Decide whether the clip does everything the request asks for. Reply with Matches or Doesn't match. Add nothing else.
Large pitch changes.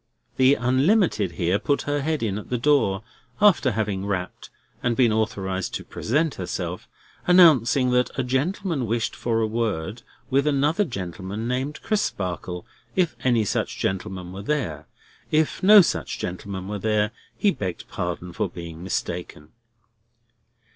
Matches